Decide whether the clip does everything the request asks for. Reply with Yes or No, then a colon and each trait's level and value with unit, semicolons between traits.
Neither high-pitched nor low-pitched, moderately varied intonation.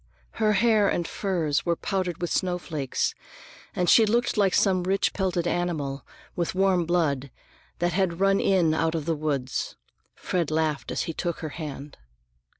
Yes: medium, 175 Hz; average, 3.4 semitones